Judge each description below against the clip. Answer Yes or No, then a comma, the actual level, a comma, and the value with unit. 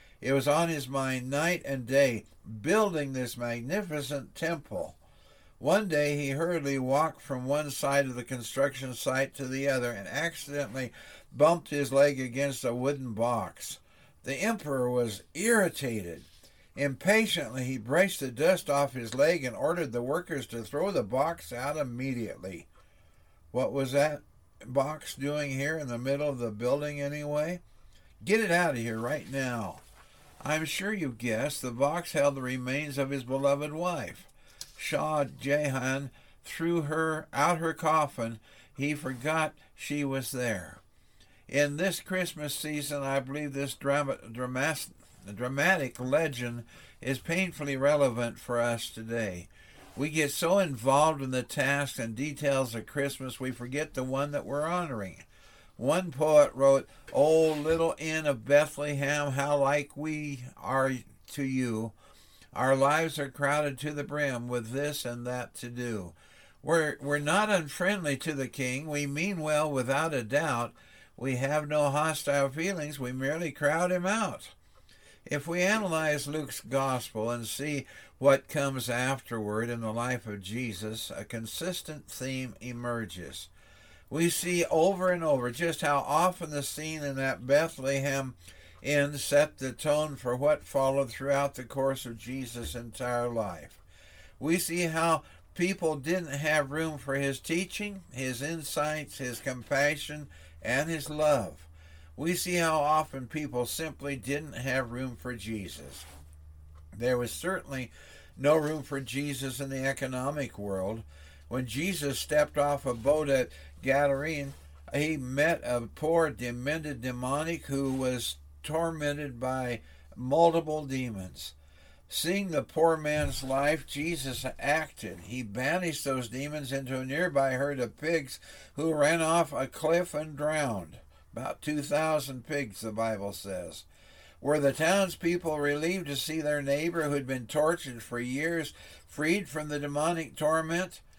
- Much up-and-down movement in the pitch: No, average, 3.7 semitones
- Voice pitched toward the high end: No, medium, 140 Hz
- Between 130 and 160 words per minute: Yes, average, 145 wpm